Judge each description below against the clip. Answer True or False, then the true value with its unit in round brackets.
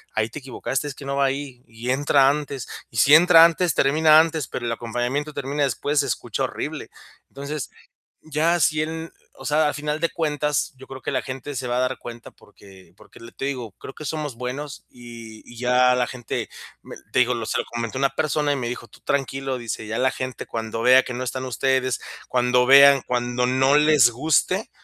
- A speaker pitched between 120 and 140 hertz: True (135 Hz)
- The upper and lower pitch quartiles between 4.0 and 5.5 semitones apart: False (3.2 semitones)